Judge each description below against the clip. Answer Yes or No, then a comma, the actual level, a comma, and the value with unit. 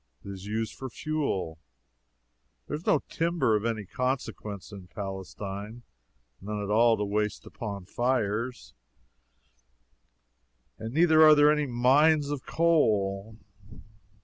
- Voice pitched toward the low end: Yes, low, 115 Hz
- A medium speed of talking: No, slow, 120 wpm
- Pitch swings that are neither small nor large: No, wide, 6.0 semitones